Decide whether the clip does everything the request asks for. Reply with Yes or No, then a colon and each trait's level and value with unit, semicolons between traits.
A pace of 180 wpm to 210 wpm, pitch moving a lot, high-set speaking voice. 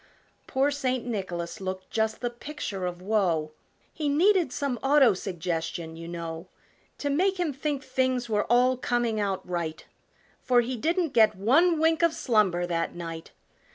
No: average, 160 wpm; wide, 7.8 semitones; high, 230 Hz